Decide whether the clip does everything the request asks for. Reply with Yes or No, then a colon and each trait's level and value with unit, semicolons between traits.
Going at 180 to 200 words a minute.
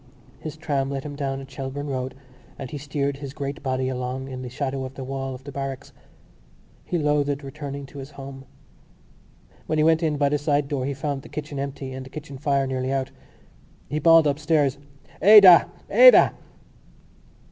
Yes: average, 185 wpm